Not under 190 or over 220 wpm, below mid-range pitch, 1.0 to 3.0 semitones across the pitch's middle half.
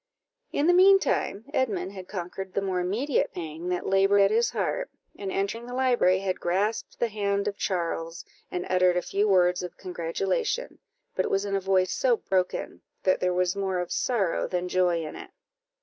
No: average, 195 wpm; high, 190 Hz; narrow, 2.4 semitones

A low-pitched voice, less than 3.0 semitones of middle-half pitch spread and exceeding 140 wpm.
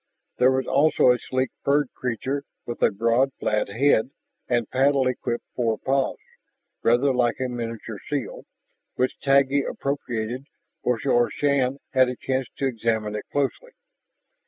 No: low, 130 Hz; narrow, 2.6 semitones; slow, 135 wpm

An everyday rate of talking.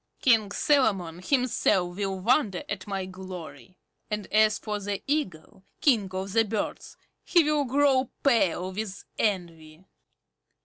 No: slow, 130 wpm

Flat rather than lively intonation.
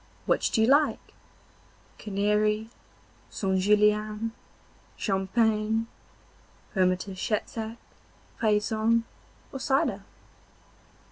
Yes: narrow, 1.8 semitones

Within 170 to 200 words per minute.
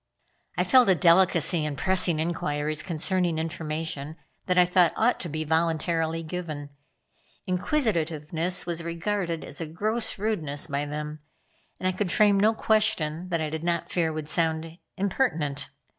No: average, 150 wpm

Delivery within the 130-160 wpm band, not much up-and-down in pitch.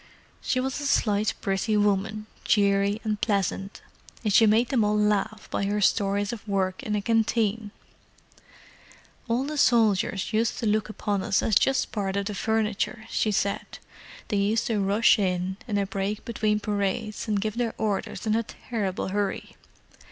No: average, 170 wpm; narrow, 1.8 semitones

